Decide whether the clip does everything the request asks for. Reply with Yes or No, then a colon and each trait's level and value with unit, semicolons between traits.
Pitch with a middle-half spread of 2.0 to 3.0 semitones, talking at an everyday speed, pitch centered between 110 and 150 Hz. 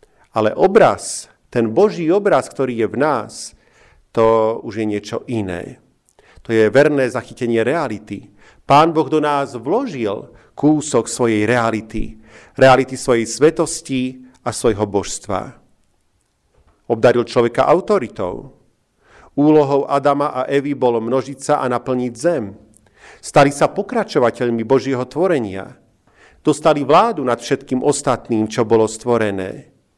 No: average, 4.1 semitones; average, 120 wpm; low, 130 Hz